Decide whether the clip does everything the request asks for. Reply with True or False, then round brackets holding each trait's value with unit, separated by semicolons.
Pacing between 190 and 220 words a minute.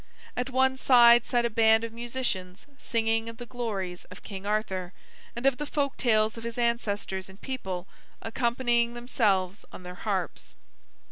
False (160 wpm)